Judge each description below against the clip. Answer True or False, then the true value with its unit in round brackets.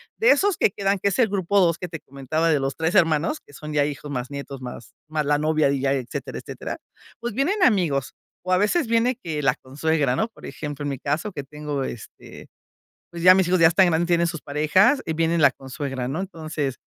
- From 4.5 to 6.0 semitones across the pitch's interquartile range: True (4.8 semitones)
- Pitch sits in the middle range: True (160 Hz)